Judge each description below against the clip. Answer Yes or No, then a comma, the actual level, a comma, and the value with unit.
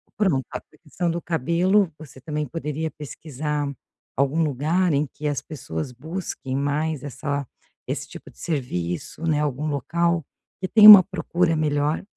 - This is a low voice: No, medium, 150 Hz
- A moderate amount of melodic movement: Yes, average, 3.1 semitones